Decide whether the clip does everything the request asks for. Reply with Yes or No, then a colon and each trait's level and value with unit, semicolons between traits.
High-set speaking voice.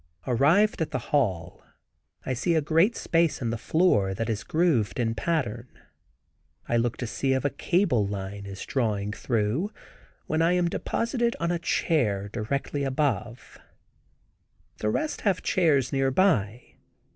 No: low, 130 Hz